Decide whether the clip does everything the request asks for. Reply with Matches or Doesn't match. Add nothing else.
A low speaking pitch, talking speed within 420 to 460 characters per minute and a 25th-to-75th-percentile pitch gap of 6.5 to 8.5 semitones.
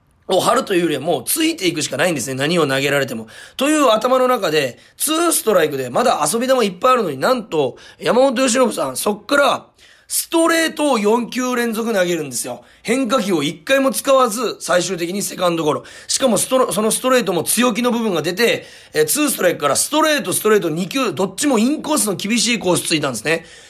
Doesn't match